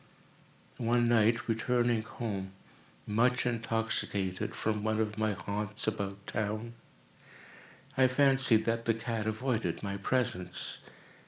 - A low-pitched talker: Yes, low, 110 Hz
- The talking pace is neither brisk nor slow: No, slow, 110 wpm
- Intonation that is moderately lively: No, narrow, 2.3 semitones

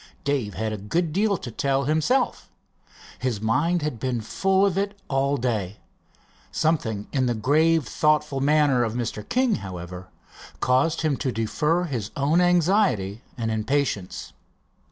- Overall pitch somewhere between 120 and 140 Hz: Yes, low, 135 Hz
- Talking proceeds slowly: No, average, 145 wpm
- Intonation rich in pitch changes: Yes, wide, 6.6 semitones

